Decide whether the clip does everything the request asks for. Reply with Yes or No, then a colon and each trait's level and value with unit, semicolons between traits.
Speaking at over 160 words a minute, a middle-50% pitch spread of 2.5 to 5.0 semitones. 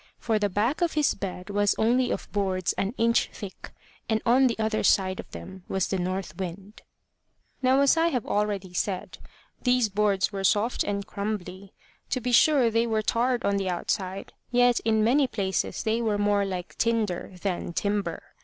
Yes: average, 180 wpm; average, 3.4 semitones